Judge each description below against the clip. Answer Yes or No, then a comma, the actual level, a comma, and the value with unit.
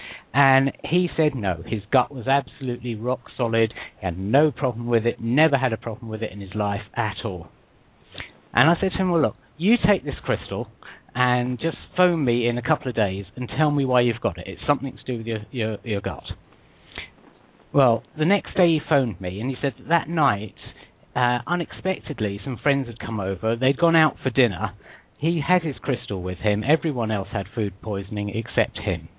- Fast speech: Yes, fast, 210 wpm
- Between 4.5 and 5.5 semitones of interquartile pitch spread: Yes, average, 5.0 semitones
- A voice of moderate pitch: No, low, 125 Hz